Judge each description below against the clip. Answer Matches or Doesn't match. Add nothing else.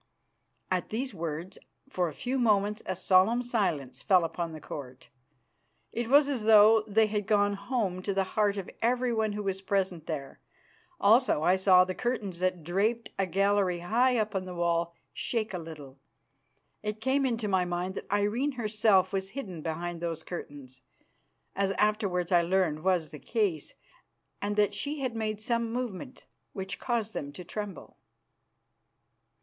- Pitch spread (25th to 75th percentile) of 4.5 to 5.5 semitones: Doesn't match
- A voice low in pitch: Doesn't match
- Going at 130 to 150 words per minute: Doesn't match